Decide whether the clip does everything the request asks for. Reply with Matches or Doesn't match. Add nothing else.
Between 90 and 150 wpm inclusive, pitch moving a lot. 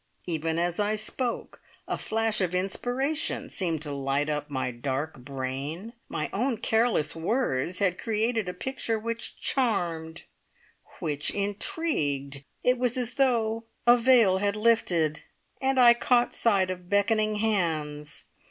Matches